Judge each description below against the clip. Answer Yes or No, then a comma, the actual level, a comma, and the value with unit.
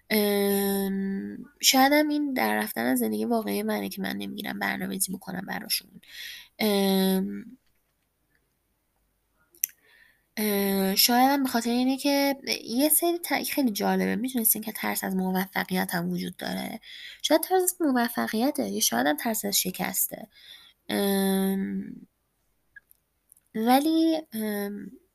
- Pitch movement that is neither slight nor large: No, wide, 5.7 semitones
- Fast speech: No, average, 120 wpm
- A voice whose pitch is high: Yes, high, 215 Hz